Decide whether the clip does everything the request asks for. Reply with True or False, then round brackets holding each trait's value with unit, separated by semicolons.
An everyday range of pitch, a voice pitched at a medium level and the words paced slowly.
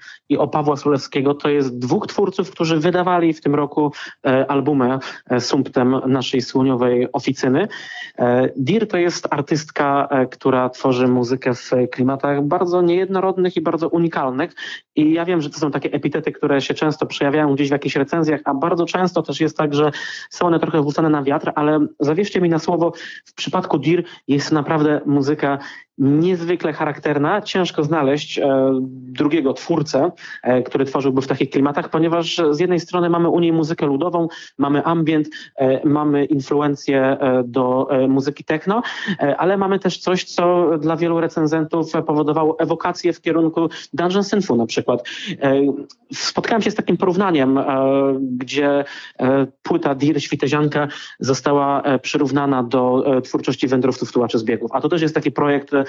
False (3.4 semitones; 150 Hz; 160 wpm)